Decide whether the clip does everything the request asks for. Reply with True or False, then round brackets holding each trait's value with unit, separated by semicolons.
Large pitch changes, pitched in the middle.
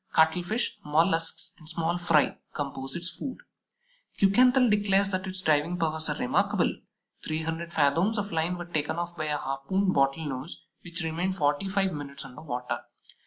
False (3.9 semitones; 165 Hz)